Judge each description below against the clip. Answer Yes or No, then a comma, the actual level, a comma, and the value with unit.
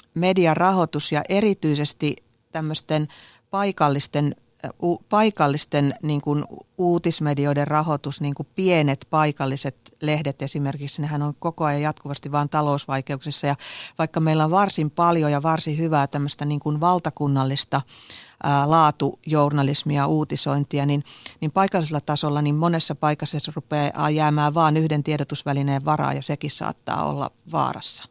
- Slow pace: No, average, 120 wpm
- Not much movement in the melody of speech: Yes, narrow, 1.7 semitones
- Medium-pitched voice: Yes, medium, 150 Hz